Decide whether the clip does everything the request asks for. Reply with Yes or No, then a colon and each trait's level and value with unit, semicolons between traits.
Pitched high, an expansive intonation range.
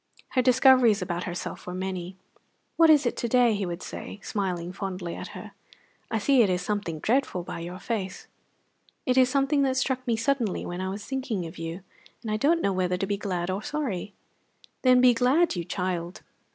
Yes: high, 205 Hz; wide, 5.9 semitones